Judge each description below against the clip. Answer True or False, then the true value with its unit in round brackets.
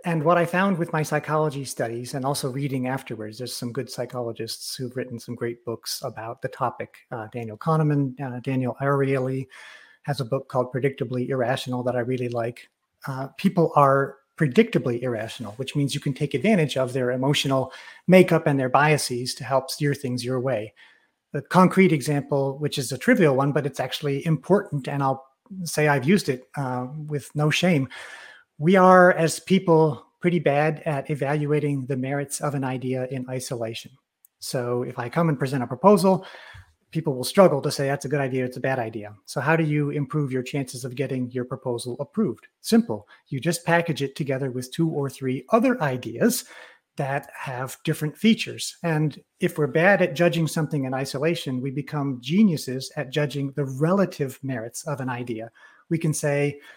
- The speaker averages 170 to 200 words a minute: True (185 wpm)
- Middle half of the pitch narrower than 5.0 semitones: True (3.5 semitones)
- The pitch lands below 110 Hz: False (140 Hz)